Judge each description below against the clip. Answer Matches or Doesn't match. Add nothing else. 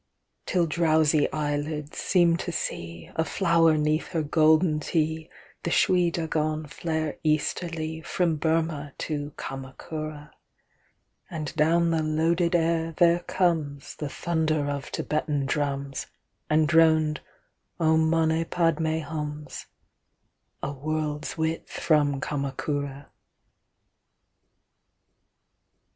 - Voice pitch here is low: Doesn't match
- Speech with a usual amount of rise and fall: Doesn't match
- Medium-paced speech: Doesn't match